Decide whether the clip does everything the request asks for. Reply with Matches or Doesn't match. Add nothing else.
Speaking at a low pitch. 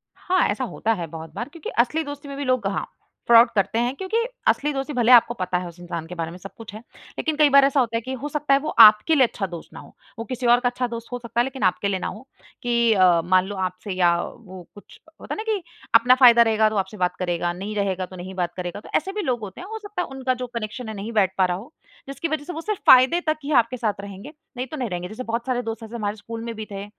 Doesn't match